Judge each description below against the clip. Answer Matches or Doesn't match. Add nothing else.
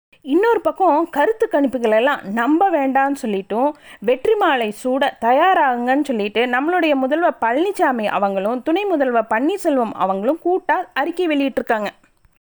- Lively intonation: Matches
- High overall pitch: Matches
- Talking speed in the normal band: Matches